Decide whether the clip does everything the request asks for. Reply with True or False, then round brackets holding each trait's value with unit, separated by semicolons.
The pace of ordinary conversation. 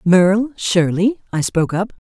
True (145 wpm)